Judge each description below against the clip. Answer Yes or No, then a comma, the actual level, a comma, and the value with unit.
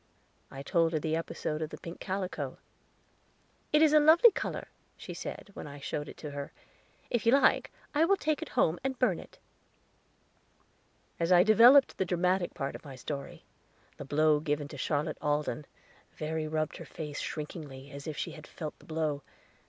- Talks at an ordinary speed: Yes, average, 180 wpm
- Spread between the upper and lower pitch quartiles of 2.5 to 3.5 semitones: No, average, 4.6 semitones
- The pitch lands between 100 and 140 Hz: No, medium, 160 Hz